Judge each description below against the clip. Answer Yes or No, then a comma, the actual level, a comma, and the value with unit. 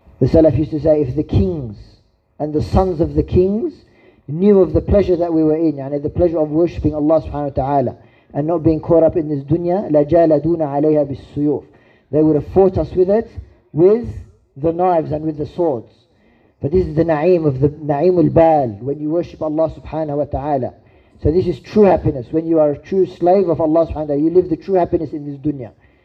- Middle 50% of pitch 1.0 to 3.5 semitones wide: Yes, average, 2.9 semitones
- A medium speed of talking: No, fast, 215 wpm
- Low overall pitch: No, medium, 155 Hz